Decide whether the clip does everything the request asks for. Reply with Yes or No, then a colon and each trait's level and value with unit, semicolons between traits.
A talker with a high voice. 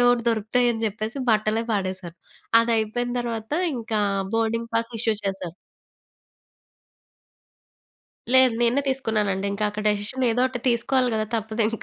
Yes: high, 225 Hz